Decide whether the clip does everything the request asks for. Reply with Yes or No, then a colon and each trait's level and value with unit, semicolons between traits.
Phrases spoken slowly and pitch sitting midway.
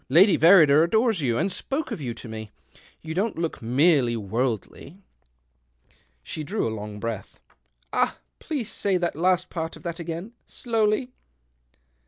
No: average, 160 wpm; medium, 165 Hz